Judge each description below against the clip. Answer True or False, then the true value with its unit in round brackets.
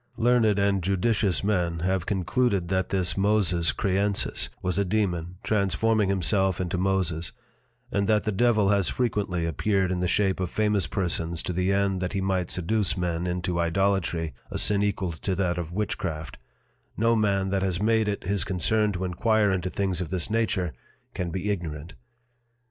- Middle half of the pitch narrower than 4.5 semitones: True (2.6 semitones)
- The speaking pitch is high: False (95 Hz)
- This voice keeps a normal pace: True (170 wpm)